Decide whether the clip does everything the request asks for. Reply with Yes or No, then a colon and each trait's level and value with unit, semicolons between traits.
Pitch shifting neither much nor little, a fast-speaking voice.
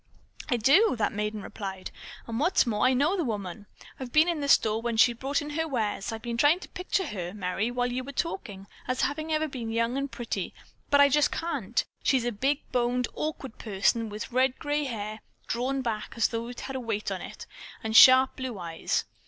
Yes: average, 4.4 semitones; fast, 220 wpm